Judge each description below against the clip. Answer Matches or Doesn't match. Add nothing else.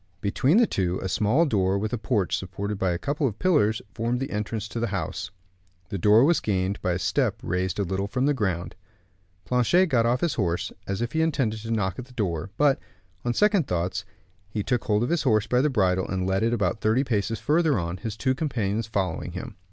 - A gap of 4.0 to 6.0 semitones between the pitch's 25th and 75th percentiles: Matches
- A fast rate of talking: Matches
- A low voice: Matches